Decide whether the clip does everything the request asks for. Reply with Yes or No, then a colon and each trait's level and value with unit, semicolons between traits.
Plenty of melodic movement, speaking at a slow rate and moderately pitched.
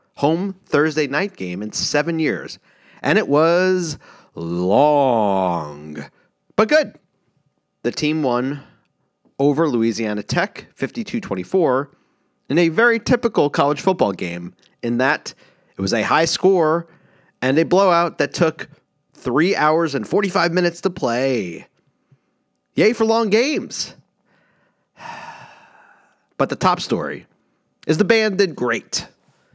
Yes: wide, 7.4 semitones; slow, 120 wpm; medium, 155 Hz